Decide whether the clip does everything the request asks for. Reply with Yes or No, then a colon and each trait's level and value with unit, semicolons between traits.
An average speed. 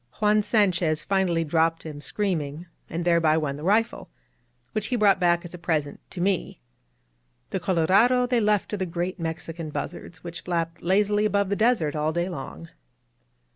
Yes: average, 170 wpm